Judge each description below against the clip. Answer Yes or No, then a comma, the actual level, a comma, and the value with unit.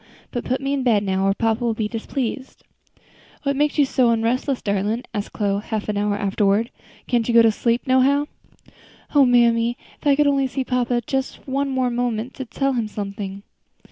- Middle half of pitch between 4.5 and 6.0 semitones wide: No, average, 3.8 semitones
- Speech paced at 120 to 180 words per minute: No, average, 200 wpm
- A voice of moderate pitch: No, high, 235 Hz